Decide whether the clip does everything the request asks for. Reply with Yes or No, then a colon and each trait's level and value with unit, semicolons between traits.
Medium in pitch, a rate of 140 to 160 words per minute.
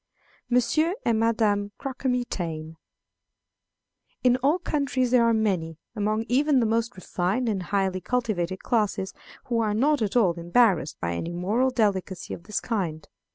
No: high, 220 Hz; average, 145 wpm